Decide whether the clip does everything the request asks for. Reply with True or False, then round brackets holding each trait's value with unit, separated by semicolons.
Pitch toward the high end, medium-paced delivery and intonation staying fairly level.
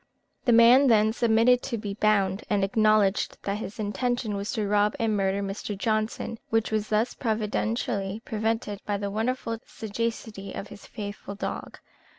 True (215 Hz; 160 wpm; 2.0 semitones)